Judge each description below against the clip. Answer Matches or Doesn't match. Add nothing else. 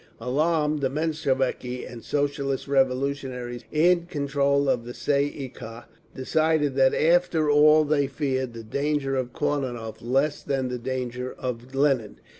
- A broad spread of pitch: Doesn't match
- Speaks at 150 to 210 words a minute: Doesn't match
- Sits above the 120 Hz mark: Matches